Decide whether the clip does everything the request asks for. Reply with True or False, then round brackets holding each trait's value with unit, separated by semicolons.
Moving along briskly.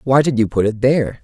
True (290 wpm)